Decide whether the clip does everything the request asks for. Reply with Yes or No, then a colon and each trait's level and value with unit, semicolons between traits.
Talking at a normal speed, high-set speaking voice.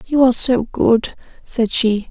Yes: average, 170 wpm; high, 240 Hz